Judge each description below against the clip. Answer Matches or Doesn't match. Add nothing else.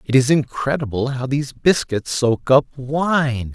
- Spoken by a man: Matches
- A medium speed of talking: Matches